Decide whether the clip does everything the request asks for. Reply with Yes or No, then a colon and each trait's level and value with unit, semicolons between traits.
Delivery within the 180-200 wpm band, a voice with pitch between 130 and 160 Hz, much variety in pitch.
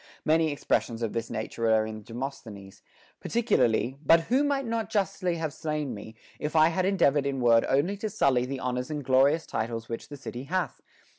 Yes: average, 190 wpm; medium, 140 Hz; wide, 6.0 semitones